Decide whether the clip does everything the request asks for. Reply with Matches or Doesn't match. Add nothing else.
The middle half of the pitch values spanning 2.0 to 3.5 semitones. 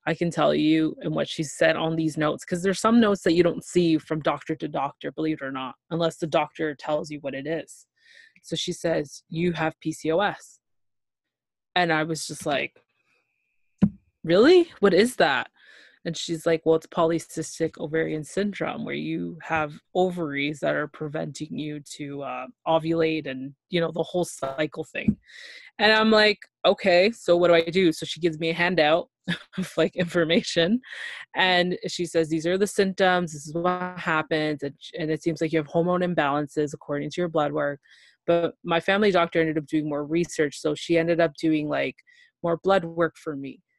Matches